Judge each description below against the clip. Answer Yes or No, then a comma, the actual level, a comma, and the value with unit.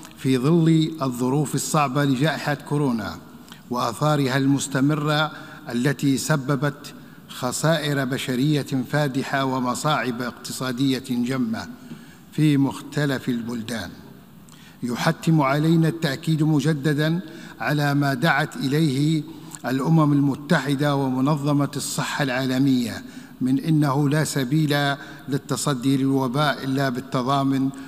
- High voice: No, medium, 140 Hz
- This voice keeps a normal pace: Yes, average, 85 wpm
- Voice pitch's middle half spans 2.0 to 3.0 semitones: Yes, narrow, 2.4 semitones